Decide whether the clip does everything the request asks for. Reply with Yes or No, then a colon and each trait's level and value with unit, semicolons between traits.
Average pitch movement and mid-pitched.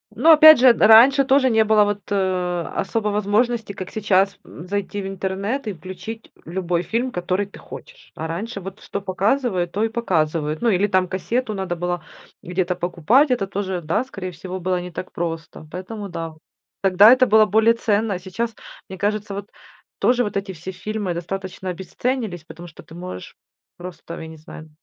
No: average, 3.7 semitones; high, 195 Hz